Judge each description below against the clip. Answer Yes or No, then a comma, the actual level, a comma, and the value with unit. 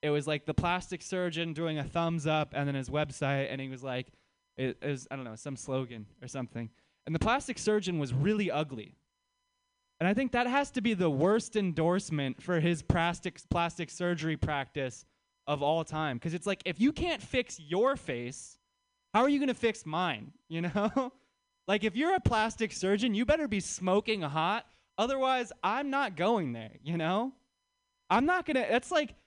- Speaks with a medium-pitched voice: Yes, medium, 180 Hz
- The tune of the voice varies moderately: No, wide, 8.9 semitones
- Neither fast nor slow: Yes, average, 195 wpm